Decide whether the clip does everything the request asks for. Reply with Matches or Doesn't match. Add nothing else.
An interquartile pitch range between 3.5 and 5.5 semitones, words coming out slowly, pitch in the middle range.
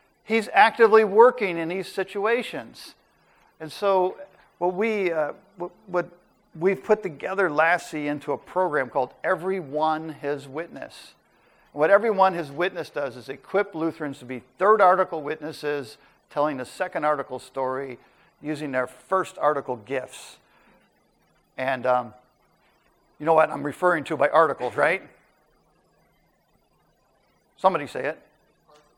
Matches